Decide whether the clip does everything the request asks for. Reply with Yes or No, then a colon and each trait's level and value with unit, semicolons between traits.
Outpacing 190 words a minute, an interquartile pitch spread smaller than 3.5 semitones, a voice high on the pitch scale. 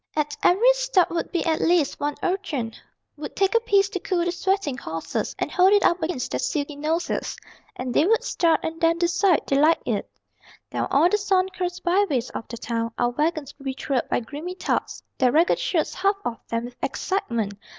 No: fast, 205 wpm; average, 5.3 semitones; very high, 330 Hz